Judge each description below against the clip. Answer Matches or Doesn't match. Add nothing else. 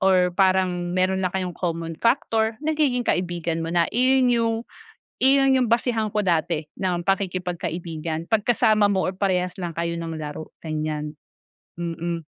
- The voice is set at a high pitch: Doesn't match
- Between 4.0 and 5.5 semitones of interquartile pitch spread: Matches